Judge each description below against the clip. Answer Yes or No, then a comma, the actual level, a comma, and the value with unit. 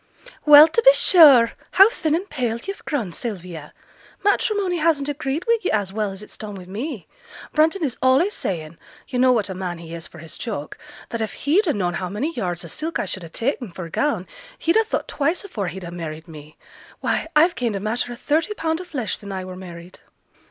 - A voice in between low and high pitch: No, high, 235 Hz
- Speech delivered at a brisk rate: Yes, fast, 225 wpm